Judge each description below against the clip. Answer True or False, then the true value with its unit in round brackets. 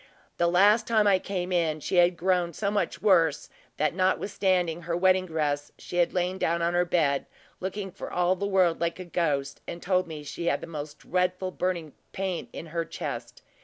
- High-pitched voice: False (175 Hz)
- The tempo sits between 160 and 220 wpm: True (200 wpm)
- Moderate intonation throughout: False (2.0 semitones)